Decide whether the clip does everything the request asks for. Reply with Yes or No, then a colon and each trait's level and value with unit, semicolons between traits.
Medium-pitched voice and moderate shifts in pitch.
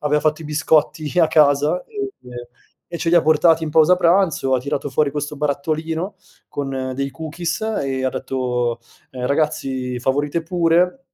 Yes: medium, 150 Hz; average, 3.1 semitones